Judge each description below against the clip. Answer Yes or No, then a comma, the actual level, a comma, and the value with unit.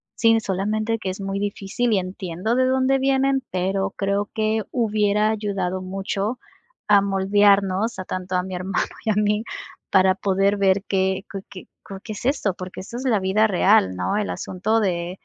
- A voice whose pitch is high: Yes, high, 200 Hz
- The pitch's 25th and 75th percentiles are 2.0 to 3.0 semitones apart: Yes, narrow, 2.4 semitones